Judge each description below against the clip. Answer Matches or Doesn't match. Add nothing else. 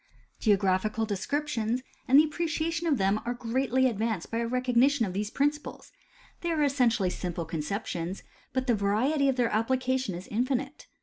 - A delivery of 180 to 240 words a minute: Doesn't match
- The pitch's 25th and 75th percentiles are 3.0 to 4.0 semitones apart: Doesn't match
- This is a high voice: Matches